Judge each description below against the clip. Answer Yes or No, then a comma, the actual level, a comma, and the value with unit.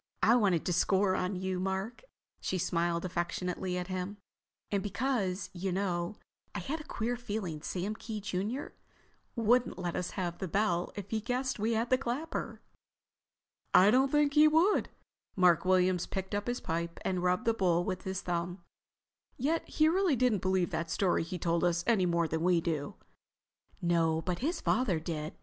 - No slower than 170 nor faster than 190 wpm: Yes, average, 175 wpm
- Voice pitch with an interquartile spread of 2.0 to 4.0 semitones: No, average, 4.6 semitones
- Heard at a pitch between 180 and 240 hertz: Yes, high, 190 Hz